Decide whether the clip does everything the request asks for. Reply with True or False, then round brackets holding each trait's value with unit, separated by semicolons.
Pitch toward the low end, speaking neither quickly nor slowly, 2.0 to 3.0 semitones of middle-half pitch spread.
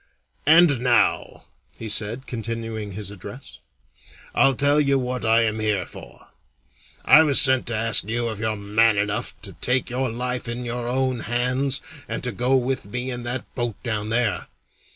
True (120 Hz; 175 wpm; 2.7 semitones)